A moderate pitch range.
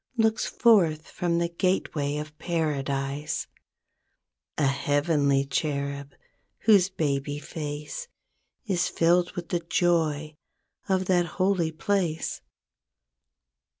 Yes: average, 3.6 semitones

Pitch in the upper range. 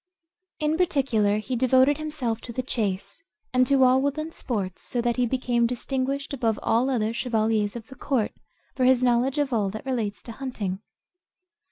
Yes: very high, 250 Hz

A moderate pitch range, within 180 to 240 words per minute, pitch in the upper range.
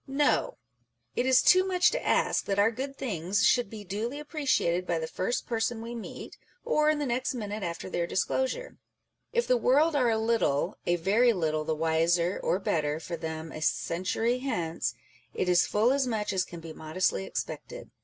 No: wide, 7.2 semitones; average, 190 wpm; high, 215 Hz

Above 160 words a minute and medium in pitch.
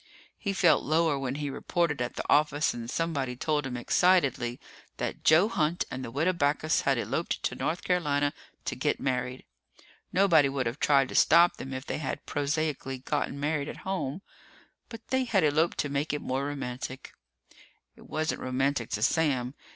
Yes: average, 175 wpm; medium, 145 Hz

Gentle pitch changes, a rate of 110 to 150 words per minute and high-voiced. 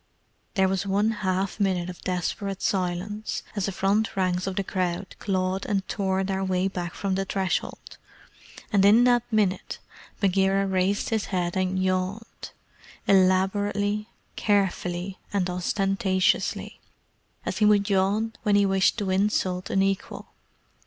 Yes: narrow, 1.5 semitones; average, 140 wpm; high, 195 Hz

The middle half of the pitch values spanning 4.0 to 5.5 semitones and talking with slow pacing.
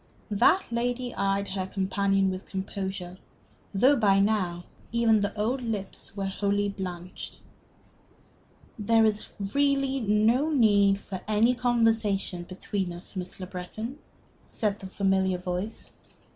No: average, 3.1 semitones; slow, 125 wpm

